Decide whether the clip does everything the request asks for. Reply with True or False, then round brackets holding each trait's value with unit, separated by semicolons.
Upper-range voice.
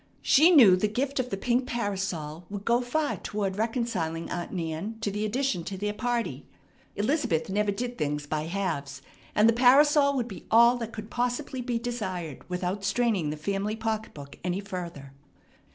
True (210 Hz)